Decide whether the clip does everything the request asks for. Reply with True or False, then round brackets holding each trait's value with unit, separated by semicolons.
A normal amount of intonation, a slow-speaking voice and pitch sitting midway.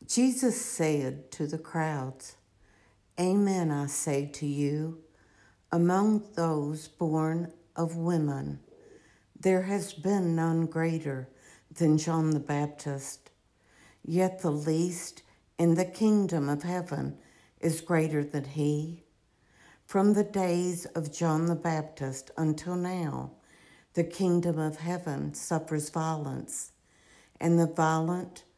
True (3.0 semitones; 115 wpm; 160 Hz)